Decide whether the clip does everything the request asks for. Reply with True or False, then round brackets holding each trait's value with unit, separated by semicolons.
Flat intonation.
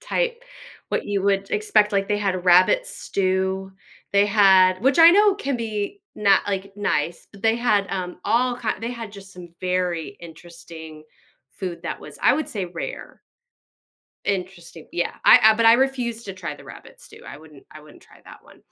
False (3.8 semitones)